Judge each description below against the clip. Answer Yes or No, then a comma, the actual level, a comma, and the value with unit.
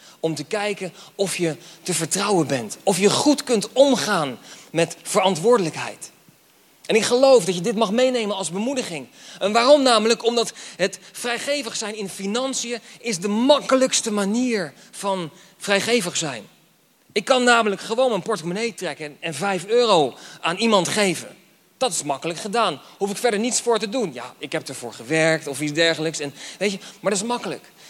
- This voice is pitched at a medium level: No, high, 205 Hz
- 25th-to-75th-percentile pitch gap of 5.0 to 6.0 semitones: Yes, wide, 5.6 semitones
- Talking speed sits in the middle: Yes, average, 170 wpm